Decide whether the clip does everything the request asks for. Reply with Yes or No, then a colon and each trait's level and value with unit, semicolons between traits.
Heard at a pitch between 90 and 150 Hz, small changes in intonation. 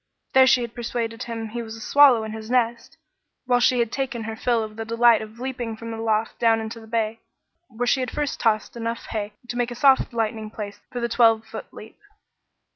No: high, 230 Hz; narrow, 1.6 semitones